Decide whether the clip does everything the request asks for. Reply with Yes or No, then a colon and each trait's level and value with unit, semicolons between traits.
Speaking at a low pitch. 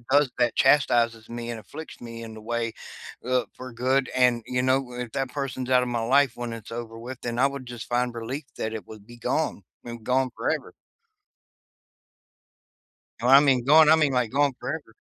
Yes: low, 125 Hz